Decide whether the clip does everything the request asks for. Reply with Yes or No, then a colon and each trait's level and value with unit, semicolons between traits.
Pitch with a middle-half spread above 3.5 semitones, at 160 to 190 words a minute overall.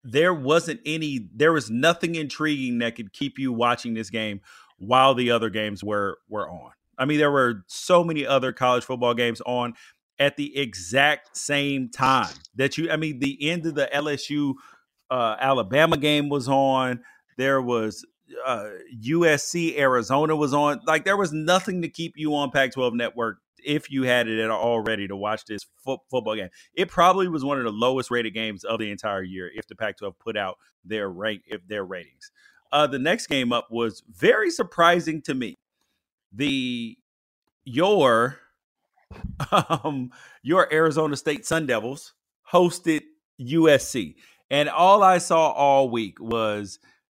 Yes: average, 4.8 semitones; average, 165 wpm